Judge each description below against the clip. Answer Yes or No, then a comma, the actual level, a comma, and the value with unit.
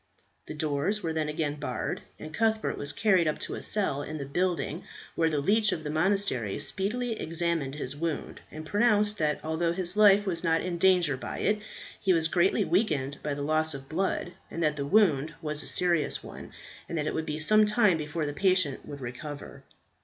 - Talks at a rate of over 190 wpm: Yes, average, 200 wpm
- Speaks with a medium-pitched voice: Yes, medium, 160 Hz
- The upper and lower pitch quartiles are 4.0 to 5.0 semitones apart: Yes, average, 4.3 semitones